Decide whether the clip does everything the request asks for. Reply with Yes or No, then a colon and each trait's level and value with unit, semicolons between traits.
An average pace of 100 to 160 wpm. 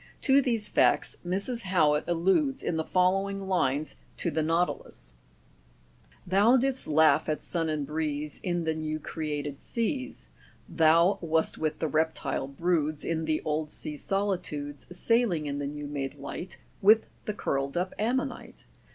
Yes: average, 150 wpm